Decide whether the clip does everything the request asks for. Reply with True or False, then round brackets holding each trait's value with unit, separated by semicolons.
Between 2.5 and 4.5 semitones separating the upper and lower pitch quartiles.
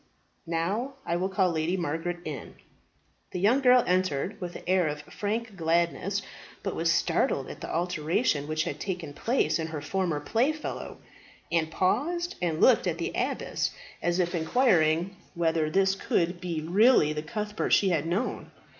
True (3.9 semitones)